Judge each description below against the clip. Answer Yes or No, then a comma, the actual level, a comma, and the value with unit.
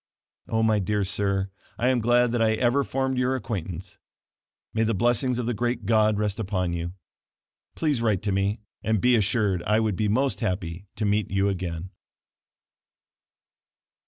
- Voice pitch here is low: Yes, low, 105 Hz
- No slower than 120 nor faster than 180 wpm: Yes, average, 165 wpm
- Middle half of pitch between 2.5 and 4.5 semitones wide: Yes, average, 3.6 semitones